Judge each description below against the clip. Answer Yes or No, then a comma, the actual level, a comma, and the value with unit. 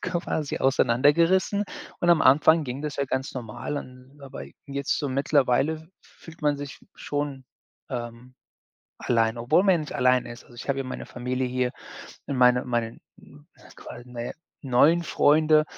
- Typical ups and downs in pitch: Yes, average, 3.5 semitones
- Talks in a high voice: No, low, 135 Hz